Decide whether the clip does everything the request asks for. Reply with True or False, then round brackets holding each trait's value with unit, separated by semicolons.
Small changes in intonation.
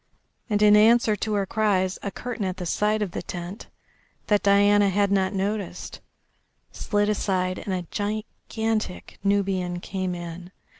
True (2.2 semitones)